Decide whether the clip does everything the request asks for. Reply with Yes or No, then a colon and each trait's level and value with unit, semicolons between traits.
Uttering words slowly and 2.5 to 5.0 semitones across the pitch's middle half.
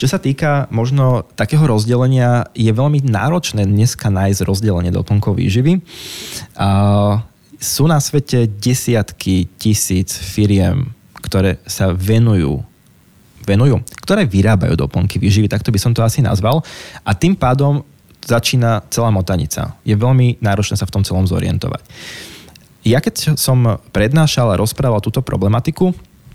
No: average, 130 wpm; average, 4.6 semitones